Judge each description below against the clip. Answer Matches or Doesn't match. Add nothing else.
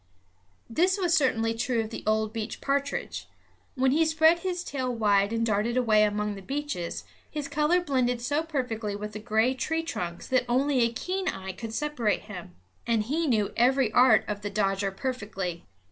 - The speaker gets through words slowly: Doesn't match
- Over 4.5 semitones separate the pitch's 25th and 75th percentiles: Matches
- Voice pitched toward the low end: Doesn't match